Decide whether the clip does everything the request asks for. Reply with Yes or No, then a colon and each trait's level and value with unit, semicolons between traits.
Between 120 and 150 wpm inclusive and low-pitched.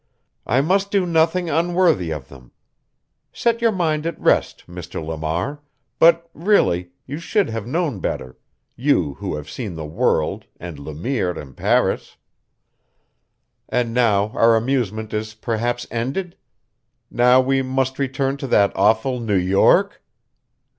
Yes: average, 140 wpm; low, 120 Hz